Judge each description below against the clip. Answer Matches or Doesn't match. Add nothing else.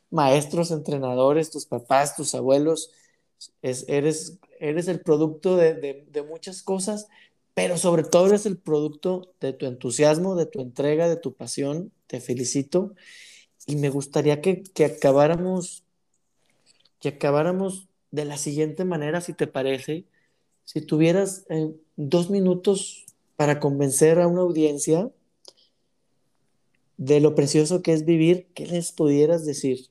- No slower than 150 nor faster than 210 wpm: Doesn't match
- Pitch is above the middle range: Doesn't match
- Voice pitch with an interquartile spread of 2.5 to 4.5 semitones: Matches